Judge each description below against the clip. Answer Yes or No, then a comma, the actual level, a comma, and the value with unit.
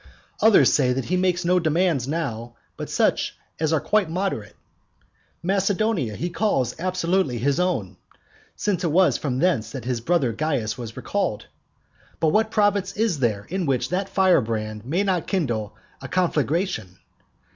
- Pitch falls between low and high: Yes, medium, 165 Hz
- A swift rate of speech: No, average, 155 wpm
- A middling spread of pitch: No, wide, 7.0 semitones